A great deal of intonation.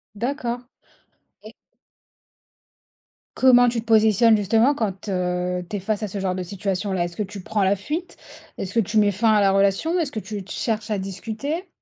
No: average, 3.2 semitones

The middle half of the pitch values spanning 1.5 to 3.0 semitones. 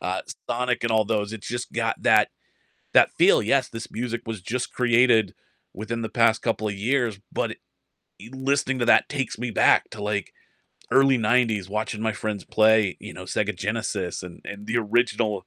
Yes: narrow, 2.6 semitones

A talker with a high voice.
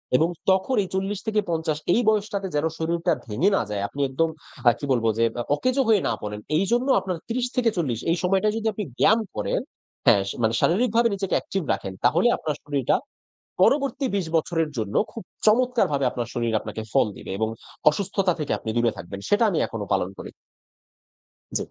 No: medium, 175 Hz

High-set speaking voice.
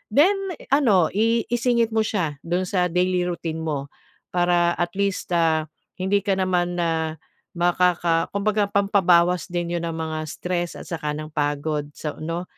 No: medium, 175 Hz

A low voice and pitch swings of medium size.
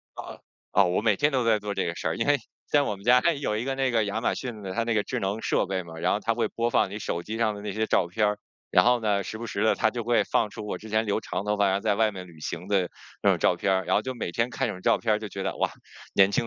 Yes: low, 105 Hz; average, 3.0 semitones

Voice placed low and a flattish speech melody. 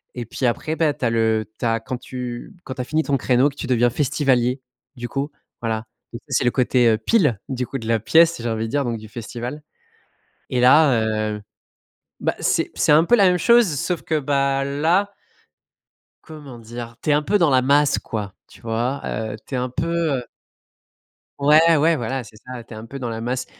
No: low, 130 Hz; average, 4.1 semitones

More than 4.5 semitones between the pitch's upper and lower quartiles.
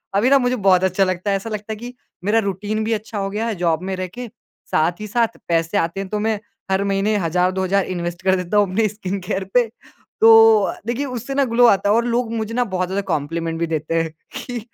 No: average, 3.6 semitones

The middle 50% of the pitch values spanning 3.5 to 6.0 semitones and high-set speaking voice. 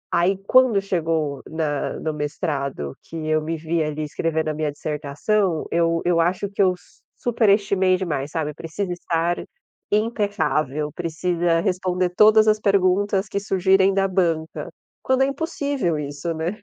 No: average, 4.1 semitones; medium, 175 Hz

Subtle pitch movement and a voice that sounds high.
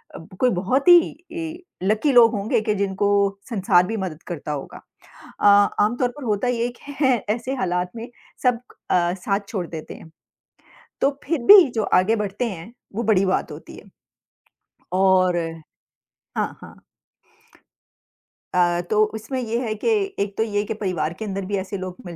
No: average, 3.9 semitones; high, 205 Hz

